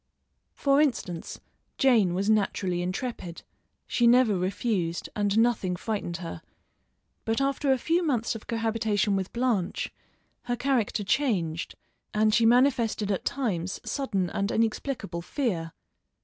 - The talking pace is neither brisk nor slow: No, slow, 125 wpm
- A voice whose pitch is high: Yes, high, 220 Hz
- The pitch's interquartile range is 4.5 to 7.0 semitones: Yes, average, 4.8 semitones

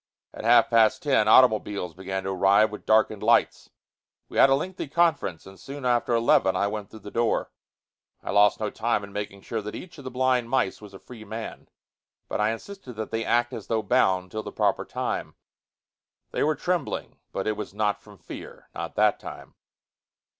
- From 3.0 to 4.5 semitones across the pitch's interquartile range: Yes, average, 3.5 semitones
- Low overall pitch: Yes, low, 110 Hz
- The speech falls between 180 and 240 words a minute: Yes, average, 195 wpm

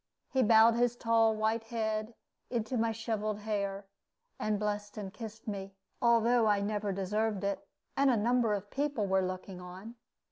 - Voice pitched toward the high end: Yes, high, 215 Hz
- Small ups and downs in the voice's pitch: Yes, narrow, 2.2 semitones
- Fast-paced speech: No, average, 165 wpm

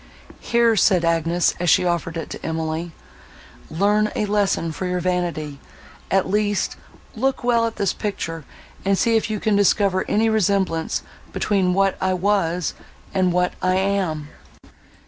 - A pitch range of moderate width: Yes, average, 3.3 semitones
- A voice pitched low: No, high, 190 Hz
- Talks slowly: No, average, 150 wpm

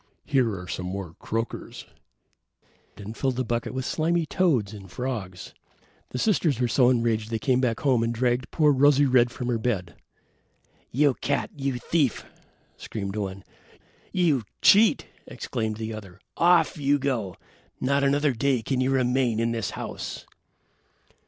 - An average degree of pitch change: Yes, average, 4.0 semitones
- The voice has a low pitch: Yes, low, 125 Hz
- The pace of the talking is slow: No, average, 160 wpm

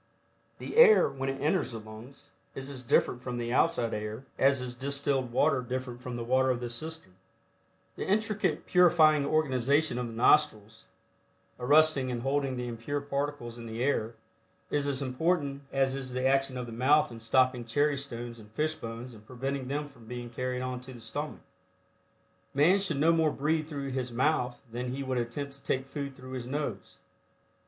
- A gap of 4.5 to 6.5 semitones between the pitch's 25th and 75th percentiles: No, average, 2.9 semitones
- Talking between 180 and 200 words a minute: Yes, average, 185 wpm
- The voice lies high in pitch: No, low, 130 Hz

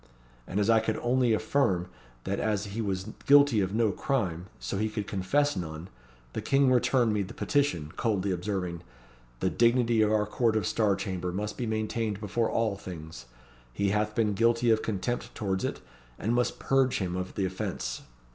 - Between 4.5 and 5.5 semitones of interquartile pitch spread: No, average, 3.6 semitones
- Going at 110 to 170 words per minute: No, average, 185 wpm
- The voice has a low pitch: Yes, low, 105 Hz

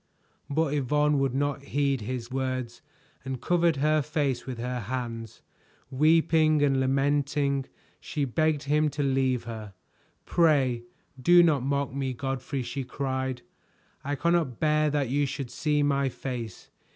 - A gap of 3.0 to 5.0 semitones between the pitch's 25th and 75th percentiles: No, narrow, 2.5 semitones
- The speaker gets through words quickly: No, average, 140 wpm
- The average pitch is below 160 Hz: Yes, medium, 140 Hz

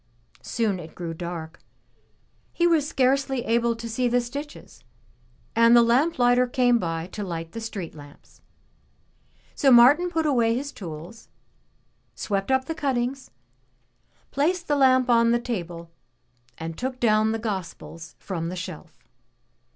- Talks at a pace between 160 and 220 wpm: No, average, 145 wpm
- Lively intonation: Yes, wide, 6.3 semitones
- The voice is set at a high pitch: Yes, high, 235 Hz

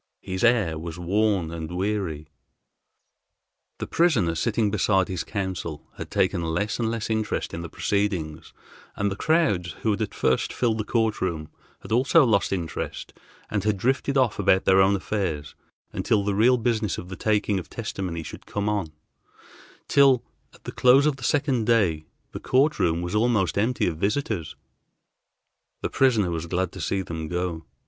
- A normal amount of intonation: Yes, average, 4.6 semitones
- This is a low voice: Yes, low, 100 Hz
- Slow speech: No, average, 170 wpm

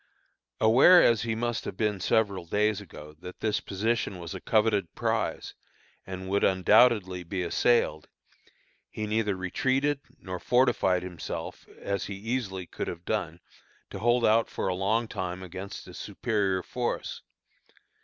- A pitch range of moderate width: Yes, average, 3.5 semitones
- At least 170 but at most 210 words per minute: No, average, 145 wpm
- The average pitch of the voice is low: Yes, low, 100 Hz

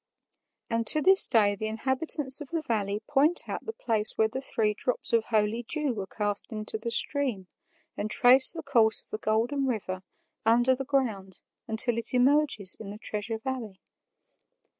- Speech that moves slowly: No, average, 175 wpm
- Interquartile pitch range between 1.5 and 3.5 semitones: No, average, 4.0 semitones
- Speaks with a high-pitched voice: Yes, high, 230 Hz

